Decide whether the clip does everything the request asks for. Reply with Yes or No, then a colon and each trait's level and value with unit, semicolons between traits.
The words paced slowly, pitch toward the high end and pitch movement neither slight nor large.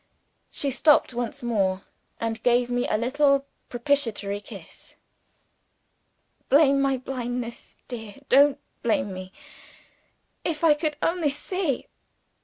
Yes: slow, 110 wpm; very high, 250 Hz; average, 3.9 semitones